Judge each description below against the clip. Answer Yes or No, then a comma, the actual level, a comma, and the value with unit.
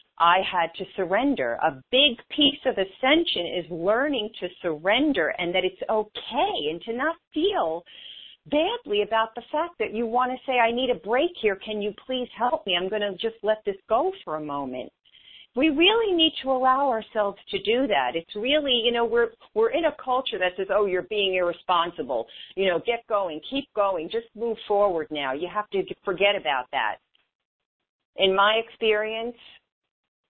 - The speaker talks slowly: No, average, 185 wpm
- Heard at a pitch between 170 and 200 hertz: No, high, 215 Hz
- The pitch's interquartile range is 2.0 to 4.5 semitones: No, wide, 5.5 semitones